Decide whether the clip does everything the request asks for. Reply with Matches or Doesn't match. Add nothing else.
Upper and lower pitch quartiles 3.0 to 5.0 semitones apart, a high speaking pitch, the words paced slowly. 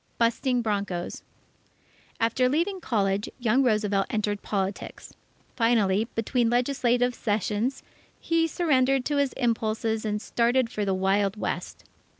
Matches